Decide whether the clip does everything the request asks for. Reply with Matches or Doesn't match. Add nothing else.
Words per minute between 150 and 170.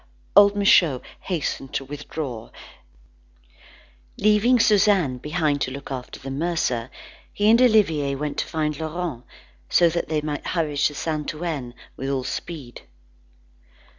Doesn't match